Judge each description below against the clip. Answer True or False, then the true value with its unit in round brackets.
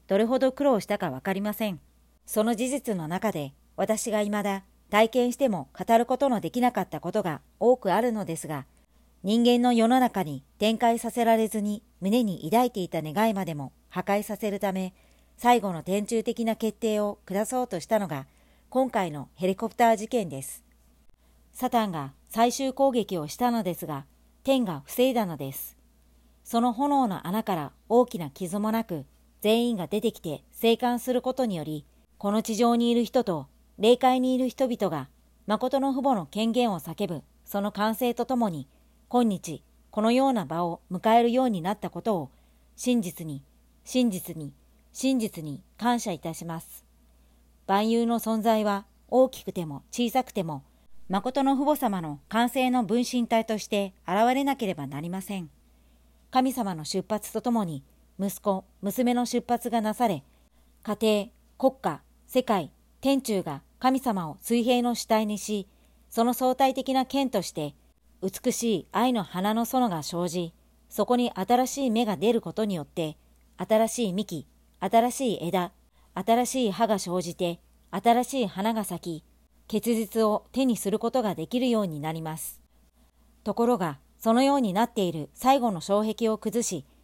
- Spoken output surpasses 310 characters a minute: False (295 characters per minute)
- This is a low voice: False (215 Hz)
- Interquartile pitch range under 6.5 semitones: True (5.5 semitones)